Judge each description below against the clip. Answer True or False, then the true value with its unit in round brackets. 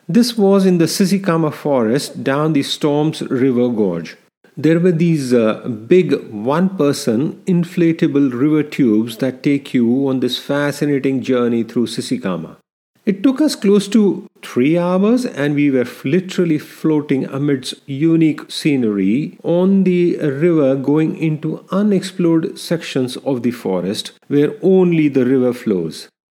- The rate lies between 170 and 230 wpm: False (135 wpm)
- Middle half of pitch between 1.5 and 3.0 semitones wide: False (5.1 semitones)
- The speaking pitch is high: False (150 Hz)